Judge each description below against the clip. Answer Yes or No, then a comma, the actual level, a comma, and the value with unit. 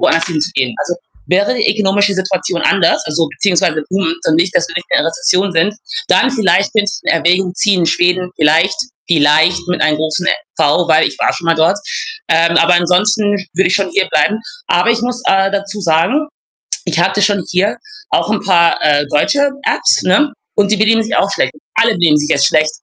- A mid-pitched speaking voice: Yes, medium, 180 Hz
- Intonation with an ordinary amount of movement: Yes, average, 3.6 semitones